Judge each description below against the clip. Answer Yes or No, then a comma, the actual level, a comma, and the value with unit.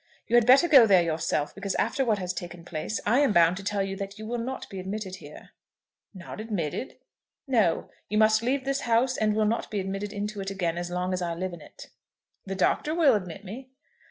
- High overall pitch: Yes, high, 200 Hz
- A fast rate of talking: Yes, fast, 225 wpm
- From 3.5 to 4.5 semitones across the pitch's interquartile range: Yes, average, 4.2 semitones